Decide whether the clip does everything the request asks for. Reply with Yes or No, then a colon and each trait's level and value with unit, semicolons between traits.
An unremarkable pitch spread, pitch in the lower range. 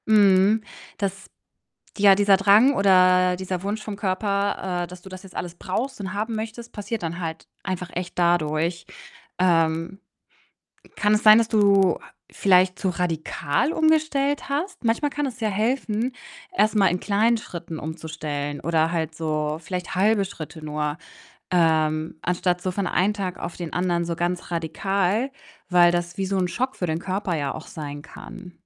No: average, 3.5 semitones; medium, 185 Hz